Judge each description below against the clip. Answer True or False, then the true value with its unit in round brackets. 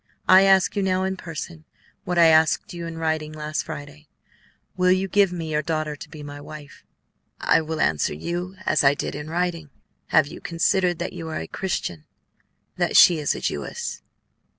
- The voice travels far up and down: False (2.9 semitones)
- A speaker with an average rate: True (190 wpm)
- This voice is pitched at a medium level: True (160 Hz)